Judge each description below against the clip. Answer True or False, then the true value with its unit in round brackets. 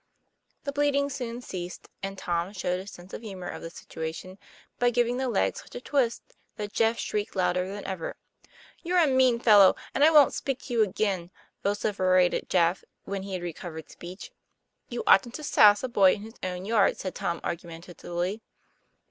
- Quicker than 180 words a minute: True (190 wpm)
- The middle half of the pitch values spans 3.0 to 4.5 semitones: False (4.9 semitones)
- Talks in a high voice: True (200 Hz)